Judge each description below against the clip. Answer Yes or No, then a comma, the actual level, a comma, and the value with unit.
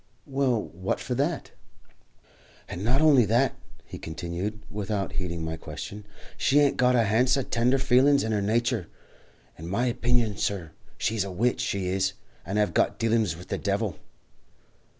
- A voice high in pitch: No, low, 110 Hz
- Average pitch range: Yes, average, 4.5 semitones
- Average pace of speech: Yes, average, 170 wpm